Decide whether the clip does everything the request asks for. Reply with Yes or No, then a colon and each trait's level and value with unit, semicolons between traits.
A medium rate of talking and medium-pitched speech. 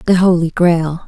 Yes: average, 165 wpm; medium, 170 Hz